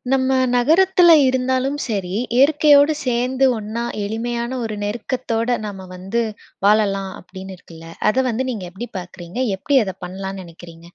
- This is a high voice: Yes, high, 230 Hz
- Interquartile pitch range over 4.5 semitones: Yes, average, 5.2 semitones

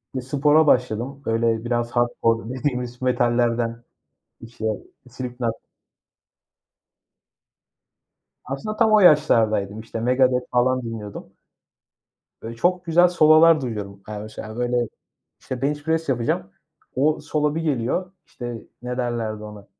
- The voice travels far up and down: No, average, 4.1 semitones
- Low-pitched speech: Yes, low, 125 Hz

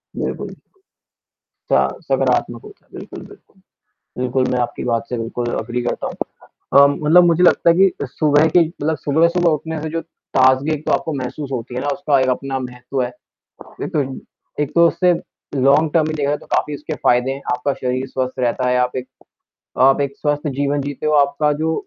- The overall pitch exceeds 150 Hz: No, medium, 140 Hz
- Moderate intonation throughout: Yes, average, 3.4 semitones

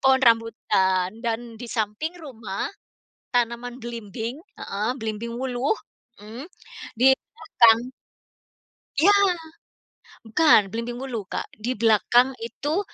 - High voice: Yes, high, 235 Hz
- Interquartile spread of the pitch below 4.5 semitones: Yes, average, 2.9 semitones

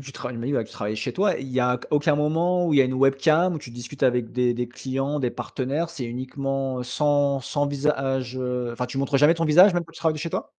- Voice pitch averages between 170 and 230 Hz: No, low, 135 Hz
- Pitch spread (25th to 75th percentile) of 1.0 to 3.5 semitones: Yes, average, 3.2 semitones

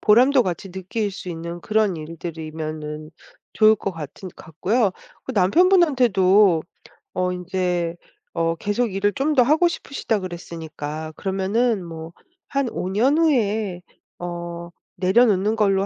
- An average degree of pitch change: Yes, average, 4.7 semitones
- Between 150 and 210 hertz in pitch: Yes, high, 190 Hz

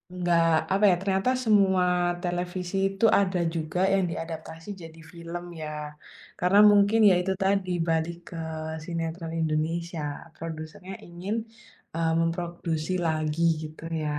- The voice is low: No, medium, 170 Hz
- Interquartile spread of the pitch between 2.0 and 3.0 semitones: Yes, narrow, 2.4 semitones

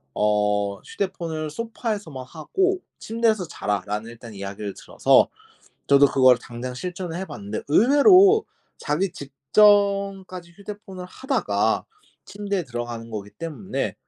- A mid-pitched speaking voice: Yes, medium, 165 Hz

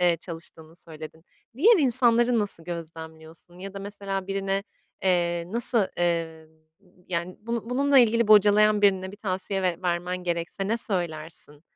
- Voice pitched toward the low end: No, medium, 185 Hz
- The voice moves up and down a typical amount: Yes, average, 3.9 semitones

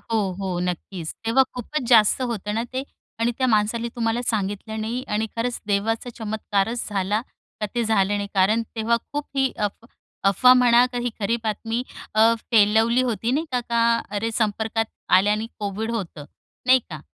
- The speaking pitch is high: Yes, high, 225 Hz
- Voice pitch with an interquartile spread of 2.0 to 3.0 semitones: Yes, narrow, 2.4 semitones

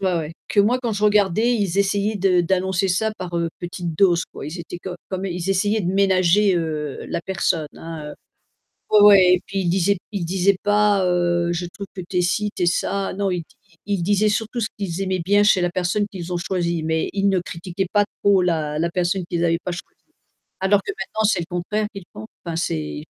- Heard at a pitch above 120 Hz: Yes, medium, 185 Hz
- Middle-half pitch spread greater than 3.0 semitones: No, average, 2.7 semitones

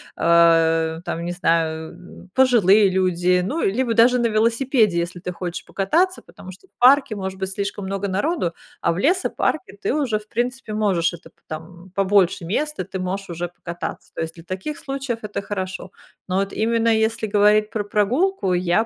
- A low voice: No, high, 195 Hz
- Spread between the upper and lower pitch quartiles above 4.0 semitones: Yes, average, 4.6 semitones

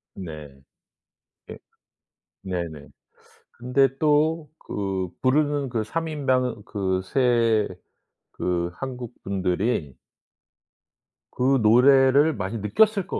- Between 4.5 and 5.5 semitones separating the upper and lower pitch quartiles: No, wide, 6.4 semitones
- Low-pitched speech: Yes, low, 120 Hz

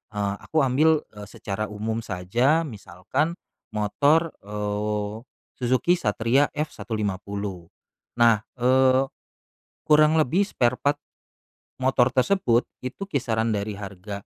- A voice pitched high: No, low, 120 Hz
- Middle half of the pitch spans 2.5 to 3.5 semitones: No, wide, 5.6 semitones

